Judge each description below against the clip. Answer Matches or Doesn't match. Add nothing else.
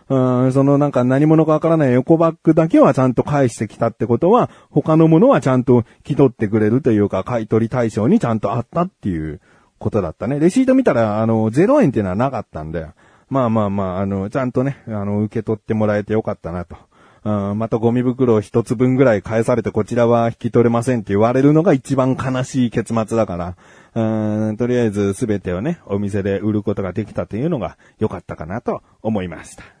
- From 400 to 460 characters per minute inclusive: Matches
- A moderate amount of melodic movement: Matches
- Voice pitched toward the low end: Matches